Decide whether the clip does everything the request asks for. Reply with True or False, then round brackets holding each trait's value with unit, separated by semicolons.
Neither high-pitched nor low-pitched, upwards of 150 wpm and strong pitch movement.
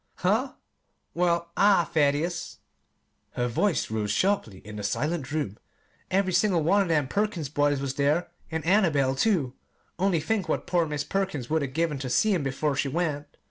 False (160 Hz; 175 wpm; 4.8 semitones)